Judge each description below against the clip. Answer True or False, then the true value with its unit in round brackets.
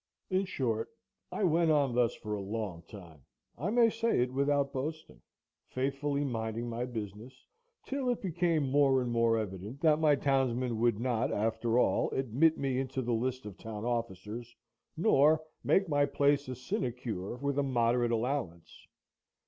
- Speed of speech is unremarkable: True (160 wpm)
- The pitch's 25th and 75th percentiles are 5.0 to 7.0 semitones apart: False (4.0 semitones)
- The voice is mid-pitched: False (130 Hz)